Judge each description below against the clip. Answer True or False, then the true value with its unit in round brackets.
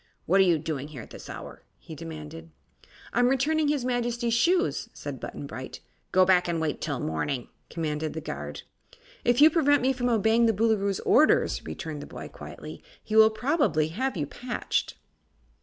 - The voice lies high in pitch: True (210 Hz)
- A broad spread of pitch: True (7.6 semitones)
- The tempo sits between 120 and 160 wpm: False (175 wpm)